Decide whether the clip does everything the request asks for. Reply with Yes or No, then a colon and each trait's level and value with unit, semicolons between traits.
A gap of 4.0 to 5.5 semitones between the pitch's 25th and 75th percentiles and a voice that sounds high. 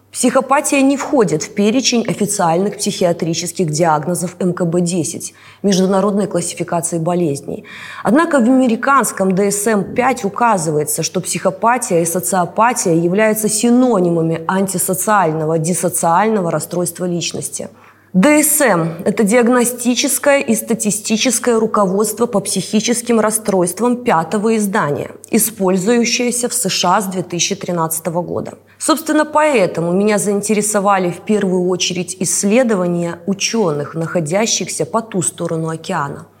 Yes: average, 4.4 semitones; high, 195 Hz